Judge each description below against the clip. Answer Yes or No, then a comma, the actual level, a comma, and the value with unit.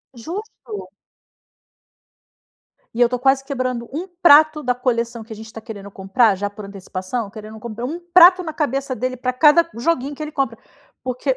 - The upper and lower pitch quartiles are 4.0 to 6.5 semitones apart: Yes, average, 4.5 semitones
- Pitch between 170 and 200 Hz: No, very high, 250 Hz